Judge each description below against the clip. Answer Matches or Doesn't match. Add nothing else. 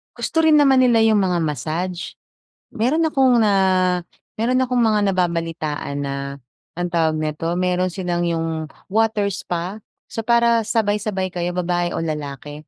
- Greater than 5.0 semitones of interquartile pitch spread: Matches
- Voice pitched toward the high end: Doesn't match